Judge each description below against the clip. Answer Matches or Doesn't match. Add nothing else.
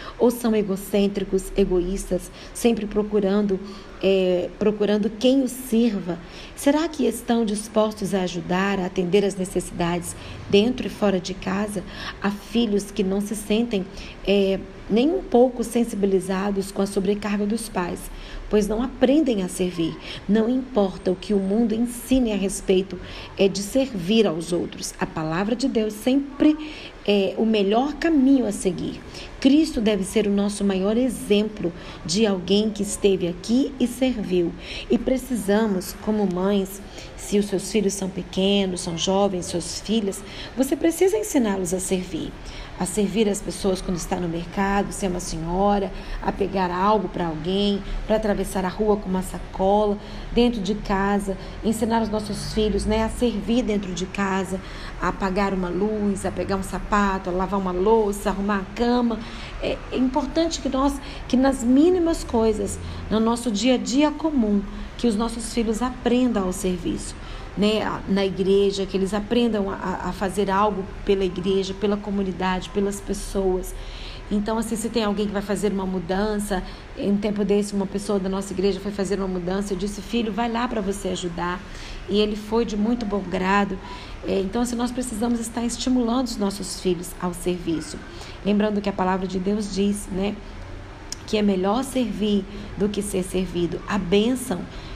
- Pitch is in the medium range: Doesn't match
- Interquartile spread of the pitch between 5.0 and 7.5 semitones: Doesn't match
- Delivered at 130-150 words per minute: Doesn't match